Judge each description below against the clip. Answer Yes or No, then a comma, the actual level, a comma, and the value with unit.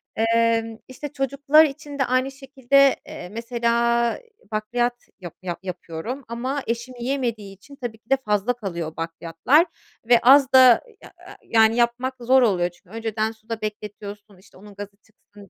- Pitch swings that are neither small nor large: Yes, average, 3.9 semitones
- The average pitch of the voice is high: Yes, high, 230 Hz